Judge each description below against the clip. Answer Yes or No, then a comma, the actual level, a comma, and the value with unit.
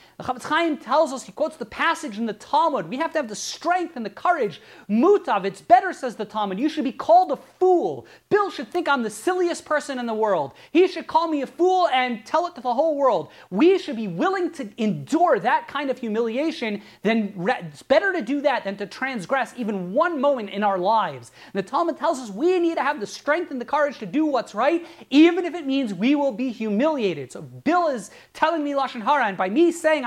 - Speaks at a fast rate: Yes, fast, 235 wpm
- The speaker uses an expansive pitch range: Yes, wide, 6.3 semitones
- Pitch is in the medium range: No, very high, 280 Hz